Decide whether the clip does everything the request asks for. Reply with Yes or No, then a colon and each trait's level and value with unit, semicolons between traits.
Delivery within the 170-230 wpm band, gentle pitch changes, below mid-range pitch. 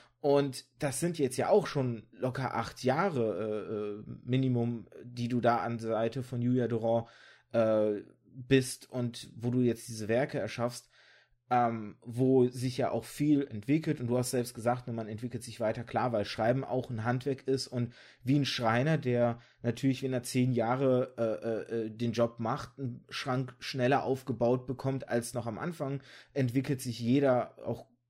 Yes: average, 175 wpm; narrow, 2.1 semitones; low, 125 Hz